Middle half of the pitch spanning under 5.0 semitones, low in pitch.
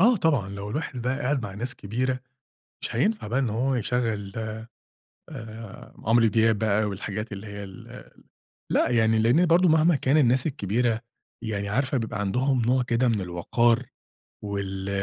Yes: average, 3.8 semitones; low, 115 Hz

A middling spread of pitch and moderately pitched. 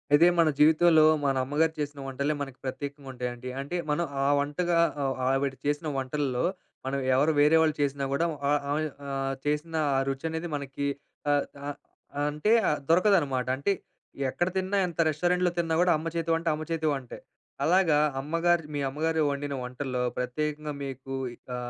Yes: average, 3.1 semitones; medium, 150 Hz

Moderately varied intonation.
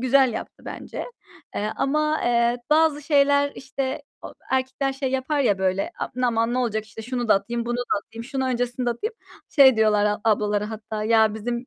Yes: average, 3.5 semitones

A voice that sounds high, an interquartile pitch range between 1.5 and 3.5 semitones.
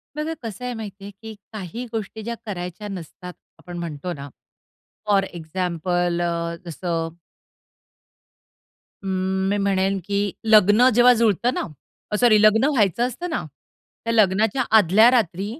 No: high, 200 Hz; average, 3.9 semitones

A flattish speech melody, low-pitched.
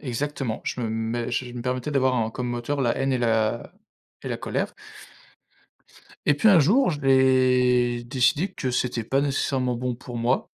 Yes: narrow, 2.1 semitones; low, 125 Hz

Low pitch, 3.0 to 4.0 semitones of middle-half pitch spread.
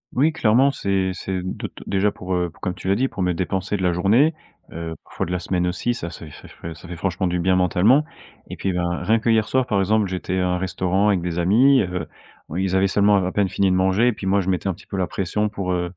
No: very low, 95 Hz; narrow, 2.5 semitones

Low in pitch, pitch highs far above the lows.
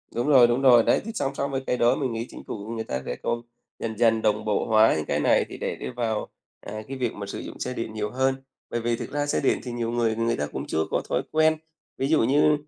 No: low, 120 Hz; average, 3.2 semitones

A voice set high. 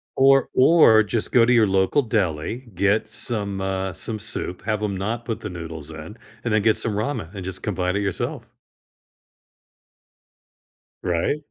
No: low, 105 Hz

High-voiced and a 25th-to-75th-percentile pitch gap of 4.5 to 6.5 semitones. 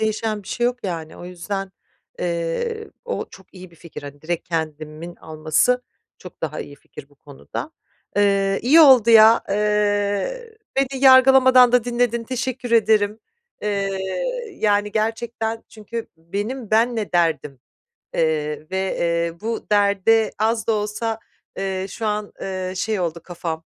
Yes: high, 205 Hz; average, 5.0 semitones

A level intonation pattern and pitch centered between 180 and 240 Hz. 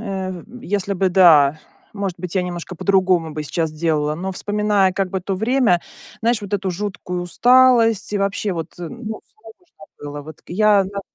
No: average, 3.1 semitones; high, 190 Hz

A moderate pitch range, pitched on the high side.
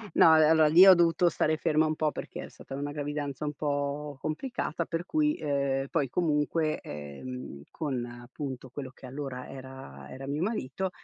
No: average, 3.0 semitones; medium, 145 Hz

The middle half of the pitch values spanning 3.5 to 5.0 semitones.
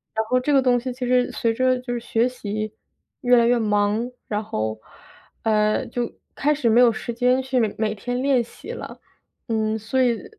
No: narrow, 2.5 semitones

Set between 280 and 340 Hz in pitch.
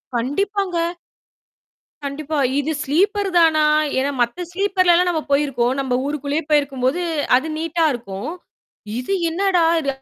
Yes: very high, 310 Hz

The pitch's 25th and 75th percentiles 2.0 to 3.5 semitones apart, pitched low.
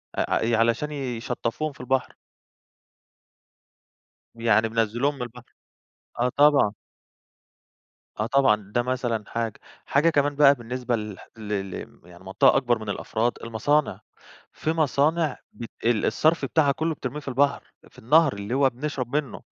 No: average, 4.0 semitones; low, 125 Hz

